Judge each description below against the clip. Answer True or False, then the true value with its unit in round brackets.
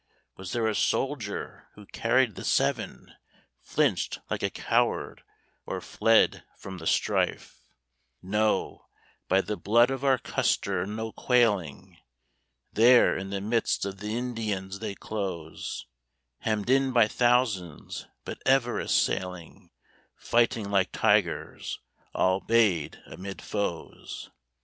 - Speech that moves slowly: True (120 wpm)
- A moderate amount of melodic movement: True (3.5 semitones)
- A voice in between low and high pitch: False (105 Hz)